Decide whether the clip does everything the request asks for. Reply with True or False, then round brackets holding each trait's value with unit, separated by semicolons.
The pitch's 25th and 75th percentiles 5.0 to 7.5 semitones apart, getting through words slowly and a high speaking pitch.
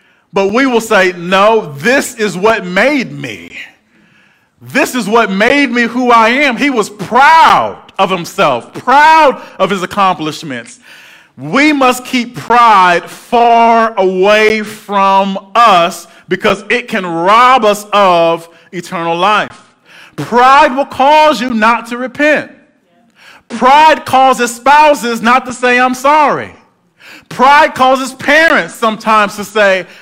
True (5.3 semitones; 130 wpm; 230 Hz)